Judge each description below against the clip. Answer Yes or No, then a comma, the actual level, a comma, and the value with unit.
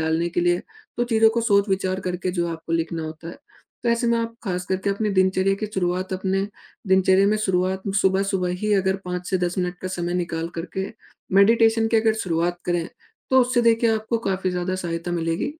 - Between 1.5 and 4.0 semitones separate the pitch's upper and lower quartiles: Yes, average, 3.3 semitones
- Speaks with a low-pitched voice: No, medium, 185 Hz